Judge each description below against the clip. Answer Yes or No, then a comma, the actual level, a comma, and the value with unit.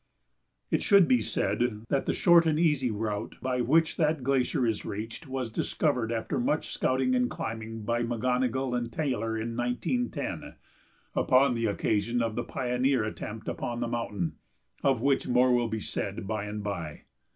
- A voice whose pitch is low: Yes, low, 120 Hz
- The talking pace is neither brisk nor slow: Yes, average, 165 wpm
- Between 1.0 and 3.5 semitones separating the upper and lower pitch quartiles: Yes, average, 2.8 semitones